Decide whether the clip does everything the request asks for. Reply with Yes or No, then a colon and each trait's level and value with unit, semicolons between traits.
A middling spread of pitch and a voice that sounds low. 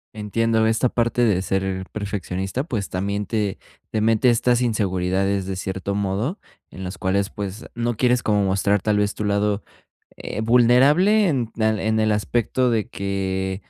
Yes: average, 3.2 semitones; low, 105 Hz